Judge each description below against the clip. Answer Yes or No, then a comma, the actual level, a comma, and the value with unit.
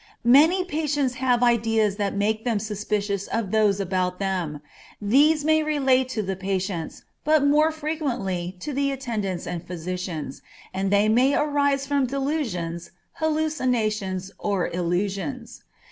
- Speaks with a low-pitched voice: No, high, 220 Hz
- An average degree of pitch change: No, wide, 6.6 semitones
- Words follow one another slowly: Yes, slow, 130 wpm